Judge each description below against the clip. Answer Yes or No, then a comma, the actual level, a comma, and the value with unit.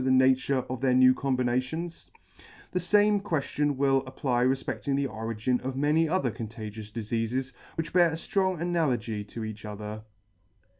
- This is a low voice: Yes, low, 130 Hz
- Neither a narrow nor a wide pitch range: Yes, average, 5.0 semitones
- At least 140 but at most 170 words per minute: Yes, average, 150 wpm